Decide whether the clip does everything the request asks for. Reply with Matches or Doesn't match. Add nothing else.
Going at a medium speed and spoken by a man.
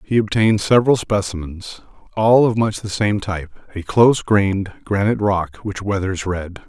Matches